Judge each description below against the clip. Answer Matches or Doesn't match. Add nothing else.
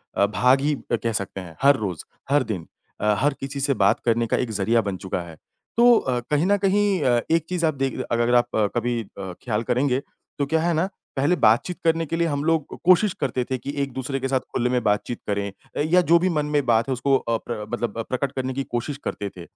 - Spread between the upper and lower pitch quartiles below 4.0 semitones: Doesn't match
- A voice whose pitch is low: Matches